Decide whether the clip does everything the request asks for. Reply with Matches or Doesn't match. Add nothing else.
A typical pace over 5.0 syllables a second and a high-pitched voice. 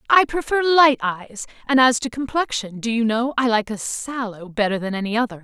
Matches